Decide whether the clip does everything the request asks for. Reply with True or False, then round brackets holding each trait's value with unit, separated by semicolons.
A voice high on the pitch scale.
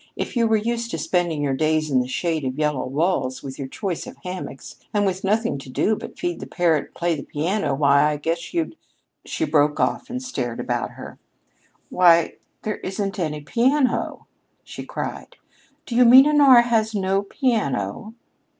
False (180 Hz)